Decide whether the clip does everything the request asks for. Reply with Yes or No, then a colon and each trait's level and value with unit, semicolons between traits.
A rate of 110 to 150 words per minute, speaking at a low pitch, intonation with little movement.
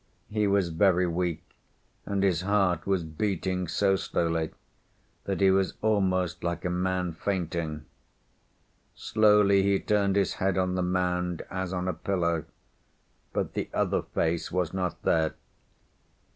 Yes: average, 140 wpm; very low, 90 Hz; narrow, 2.3 semitones